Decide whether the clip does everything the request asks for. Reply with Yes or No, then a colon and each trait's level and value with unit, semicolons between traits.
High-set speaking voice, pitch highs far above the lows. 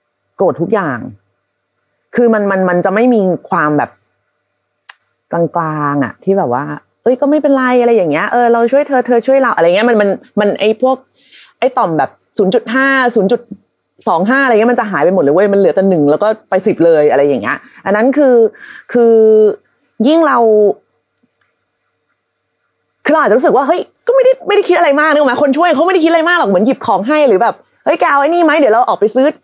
Yes: high, 235 Hz; wide, 6.1 semitones